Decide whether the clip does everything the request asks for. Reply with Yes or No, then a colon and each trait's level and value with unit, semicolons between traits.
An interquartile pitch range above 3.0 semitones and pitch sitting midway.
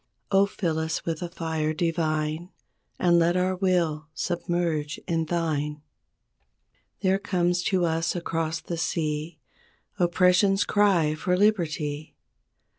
No: narrow, 2.4 semitones; medium, 170 Hz